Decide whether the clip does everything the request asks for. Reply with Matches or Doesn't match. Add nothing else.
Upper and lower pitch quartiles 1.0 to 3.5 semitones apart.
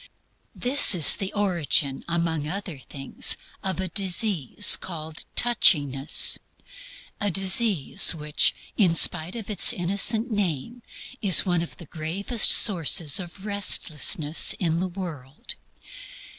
Doesn't match